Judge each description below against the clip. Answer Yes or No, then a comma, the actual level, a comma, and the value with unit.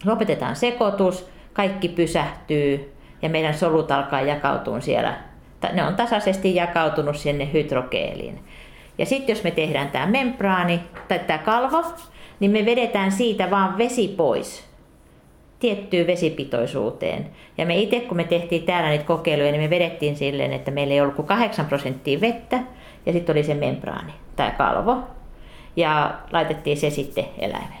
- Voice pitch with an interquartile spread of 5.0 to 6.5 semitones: Yes, wide, 5.4 semitones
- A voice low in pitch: No, medium, 170 Hz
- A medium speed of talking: Yes, average, 145 wpm